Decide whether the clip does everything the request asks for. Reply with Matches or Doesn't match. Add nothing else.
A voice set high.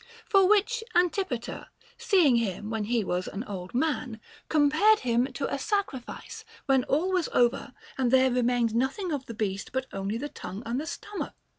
Matches